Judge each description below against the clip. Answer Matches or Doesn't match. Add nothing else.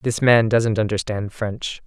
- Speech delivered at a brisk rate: Doesn't match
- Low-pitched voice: Matches